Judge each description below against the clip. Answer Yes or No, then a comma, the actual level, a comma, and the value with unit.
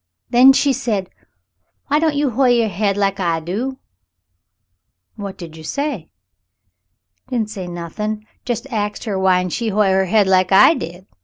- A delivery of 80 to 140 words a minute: No, average, 165 wpm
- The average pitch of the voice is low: No, high, 195 Hz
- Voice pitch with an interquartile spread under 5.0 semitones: No, wide, 5.4 semitones